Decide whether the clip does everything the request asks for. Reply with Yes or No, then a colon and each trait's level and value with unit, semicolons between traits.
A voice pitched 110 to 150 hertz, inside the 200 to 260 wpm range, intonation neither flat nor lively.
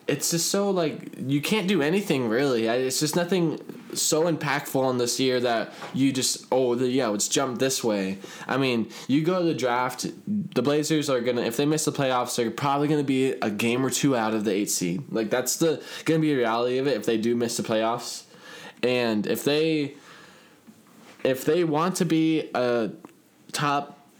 Yes: low, 135 Hz; fast, 205 wpm; average, 4.2 semitones